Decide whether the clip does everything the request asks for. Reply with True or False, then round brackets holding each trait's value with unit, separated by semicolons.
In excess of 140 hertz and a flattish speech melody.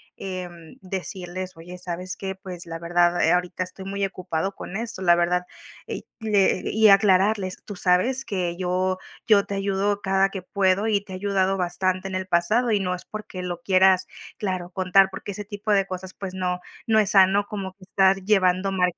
True (190 Hz; 1.6 semitones)